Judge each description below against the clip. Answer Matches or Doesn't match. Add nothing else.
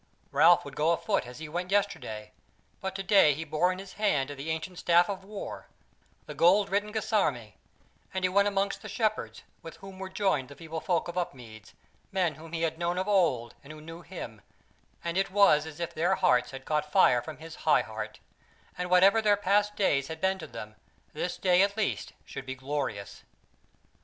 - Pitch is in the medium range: Matches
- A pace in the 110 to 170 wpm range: Doesn't match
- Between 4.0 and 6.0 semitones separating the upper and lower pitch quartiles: Matches